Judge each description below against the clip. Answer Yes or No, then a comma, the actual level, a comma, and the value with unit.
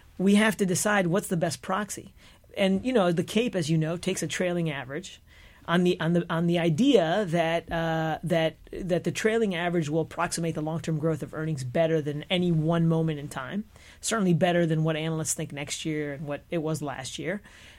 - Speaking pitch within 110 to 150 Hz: No, medium, 165 Hz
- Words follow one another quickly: Yes, fast, 210 wpm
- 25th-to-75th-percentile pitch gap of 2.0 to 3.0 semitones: Yes, narrow, 2.5 semitones